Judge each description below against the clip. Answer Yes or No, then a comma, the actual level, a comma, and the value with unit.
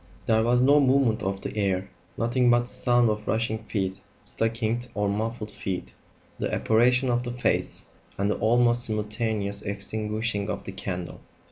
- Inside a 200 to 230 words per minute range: No, average, 160 wpm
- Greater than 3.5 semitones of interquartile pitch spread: No, average, 2.8 semitones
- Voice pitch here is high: No, low, 110 Hz